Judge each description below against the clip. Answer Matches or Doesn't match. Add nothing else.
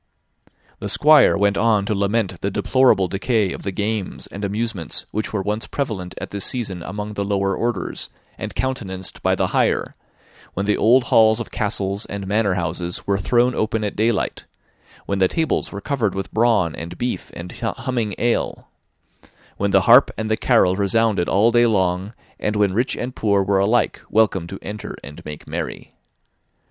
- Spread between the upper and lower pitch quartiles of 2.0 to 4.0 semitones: Matches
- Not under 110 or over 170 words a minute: Doesn't match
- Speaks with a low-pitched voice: Matches